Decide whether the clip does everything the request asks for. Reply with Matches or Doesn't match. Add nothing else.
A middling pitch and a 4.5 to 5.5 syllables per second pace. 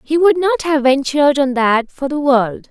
Doesn't match